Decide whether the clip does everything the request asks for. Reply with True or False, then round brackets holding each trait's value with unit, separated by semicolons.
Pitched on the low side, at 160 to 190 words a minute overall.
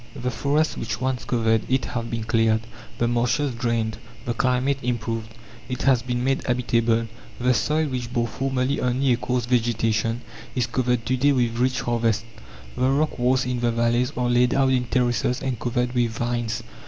True (120 Hz; 180 wpm)